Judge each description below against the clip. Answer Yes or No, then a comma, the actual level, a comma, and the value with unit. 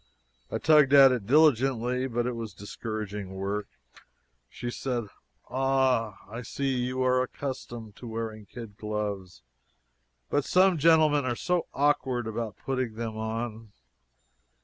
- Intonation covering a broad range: No, average, 3.6 semitones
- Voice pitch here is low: Yes, low, 120 Hz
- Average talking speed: No, slow, 130 wpm